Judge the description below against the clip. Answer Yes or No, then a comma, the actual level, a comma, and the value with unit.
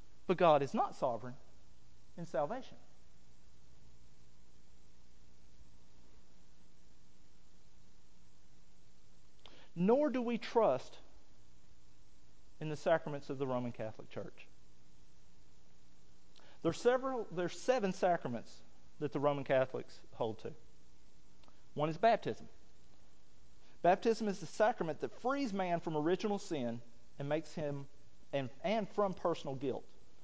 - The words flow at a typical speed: No, slow, 105 wpm